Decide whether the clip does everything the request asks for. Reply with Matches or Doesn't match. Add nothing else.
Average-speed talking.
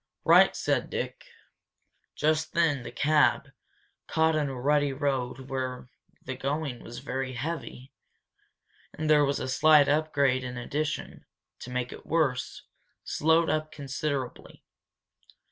Doesn't match